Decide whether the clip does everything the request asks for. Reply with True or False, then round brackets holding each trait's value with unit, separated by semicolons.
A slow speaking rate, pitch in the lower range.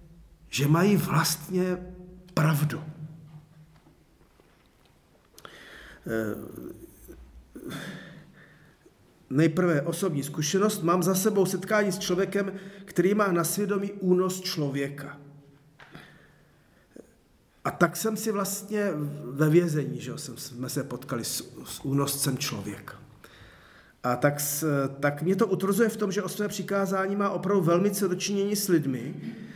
False (110 wpm; 170 Hz)